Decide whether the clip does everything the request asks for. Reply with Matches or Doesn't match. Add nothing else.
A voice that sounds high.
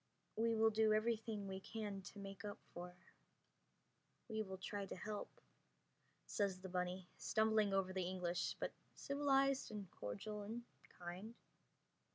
Matches